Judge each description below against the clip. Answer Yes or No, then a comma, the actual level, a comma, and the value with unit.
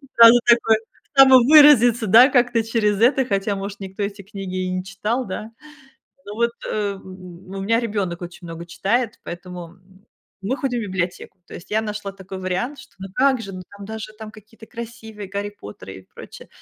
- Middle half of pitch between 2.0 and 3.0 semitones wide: No, average, 3.6 semitones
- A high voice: Yes, high, 205 Hz